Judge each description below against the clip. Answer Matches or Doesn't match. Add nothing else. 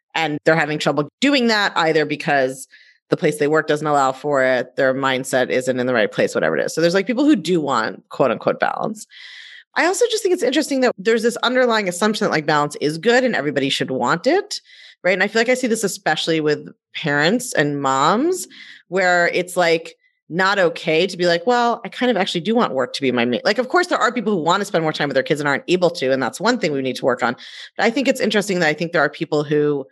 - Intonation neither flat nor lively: Doesn't match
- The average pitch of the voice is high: Doesn't match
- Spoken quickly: Matches